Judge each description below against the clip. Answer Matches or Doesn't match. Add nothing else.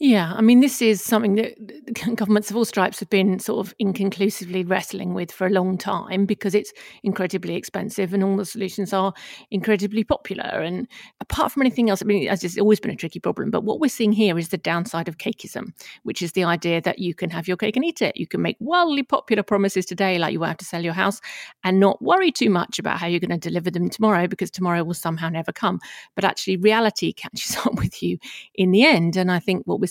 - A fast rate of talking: Matches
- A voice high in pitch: Matches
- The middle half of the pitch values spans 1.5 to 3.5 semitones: Matches